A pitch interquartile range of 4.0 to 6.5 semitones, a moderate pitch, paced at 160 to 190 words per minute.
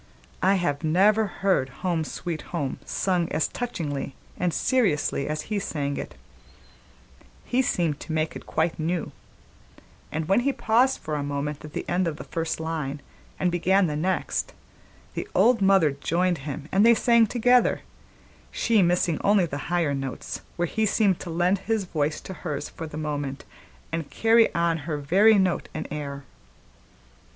Yes: average, 4.6 semitones; medium, 170 Hz; average, 165 wpm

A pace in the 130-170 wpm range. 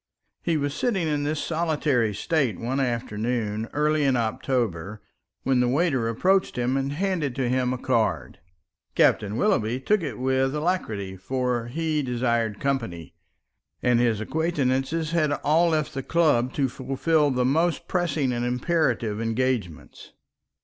Yes: average, 140 wpm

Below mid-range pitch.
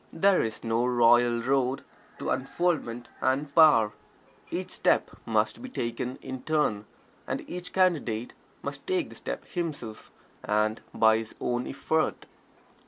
Yes: low, 125 Hz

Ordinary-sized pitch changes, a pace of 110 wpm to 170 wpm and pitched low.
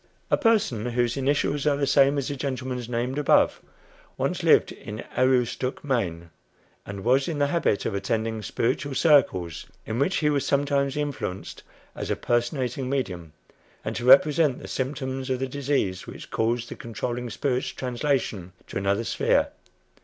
Yes: average, 3.5 semitones; average, 160 wpm; low, 130 Hz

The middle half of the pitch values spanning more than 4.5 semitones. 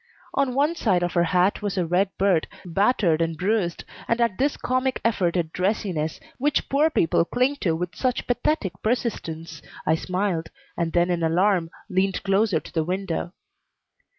Yes: wide, 5.4 semitones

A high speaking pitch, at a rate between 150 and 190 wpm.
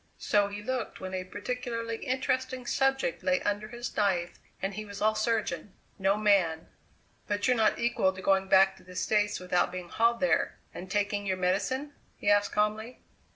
Yes: high, 205 Hz; average, 180 wpm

